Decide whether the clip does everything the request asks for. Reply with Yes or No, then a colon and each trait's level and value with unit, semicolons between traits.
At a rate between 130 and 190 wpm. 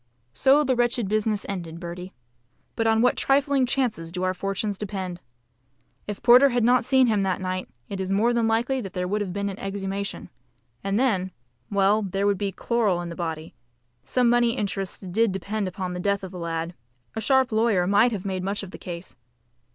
No: average, 200 wpm